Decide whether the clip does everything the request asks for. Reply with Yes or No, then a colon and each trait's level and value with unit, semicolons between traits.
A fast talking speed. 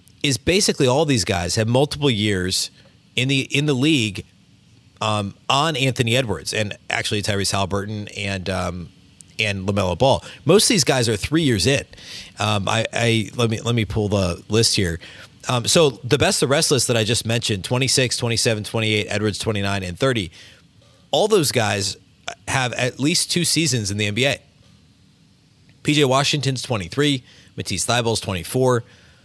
No: average, 165 wpm